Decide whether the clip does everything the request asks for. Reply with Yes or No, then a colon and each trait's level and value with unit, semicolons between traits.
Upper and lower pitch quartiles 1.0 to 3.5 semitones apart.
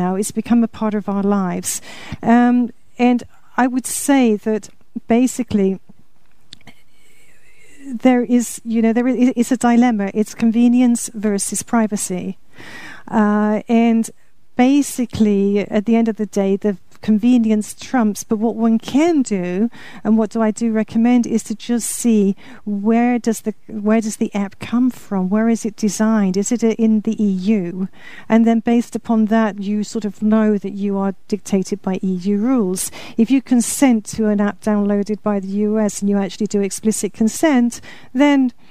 Yes: narrow, 2.5 semitones